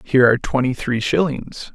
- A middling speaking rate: Yes, average, 170 wpm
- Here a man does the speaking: Yes, male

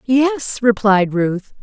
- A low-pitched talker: No, high, 225 Hz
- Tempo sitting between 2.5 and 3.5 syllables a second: Yes, 2.7 syllables/s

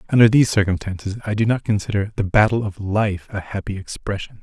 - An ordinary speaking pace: Yes, average, 190 wpm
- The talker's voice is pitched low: Yes, low, 100 Hz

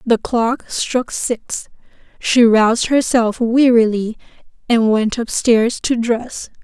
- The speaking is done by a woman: Yes, female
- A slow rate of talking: Yes, slow, 120 wpm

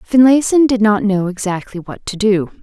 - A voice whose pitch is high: Yes, high, 215 Hz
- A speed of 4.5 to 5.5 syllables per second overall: Yes, 4.9 syllables/s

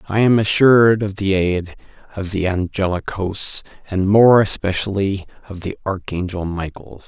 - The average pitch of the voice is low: Yes, low, 100 Hz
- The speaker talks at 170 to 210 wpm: No, average, 145 wpm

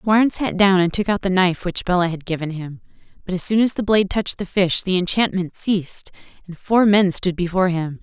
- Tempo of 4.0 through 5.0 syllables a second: No, 5.7 syllables/s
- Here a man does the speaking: No, female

